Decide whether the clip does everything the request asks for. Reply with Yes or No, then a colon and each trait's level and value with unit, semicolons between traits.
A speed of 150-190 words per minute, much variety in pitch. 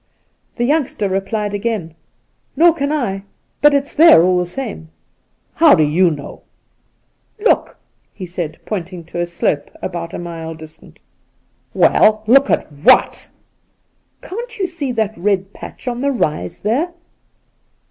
Yes: average, 160 wpm; wide, 8.2 semitones